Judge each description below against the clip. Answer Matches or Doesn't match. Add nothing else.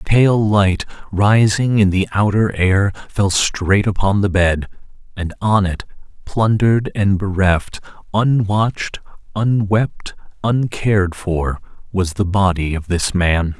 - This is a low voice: Matches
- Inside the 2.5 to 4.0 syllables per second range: Matches